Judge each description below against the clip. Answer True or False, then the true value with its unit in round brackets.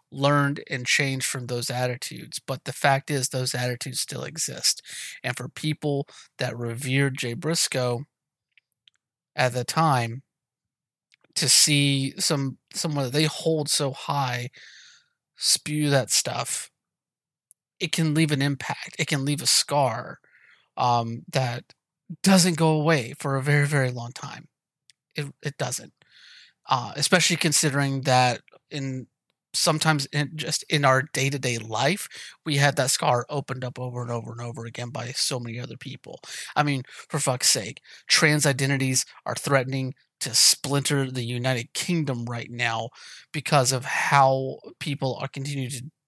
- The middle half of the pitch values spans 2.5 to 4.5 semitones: True (2.9 semitones)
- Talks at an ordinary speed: True (150 wpm)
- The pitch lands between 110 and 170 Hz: True (135 Hz)